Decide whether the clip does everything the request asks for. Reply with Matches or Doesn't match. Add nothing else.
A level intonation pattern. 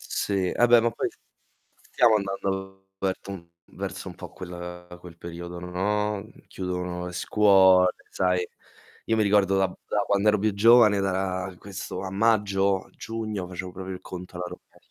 Matches